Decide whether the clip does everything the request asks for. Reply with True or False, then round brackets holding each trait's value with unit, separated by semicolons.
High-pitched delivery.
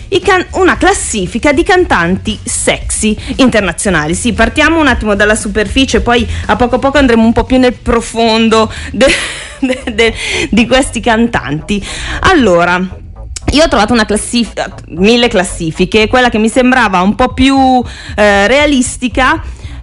True (235 Hz)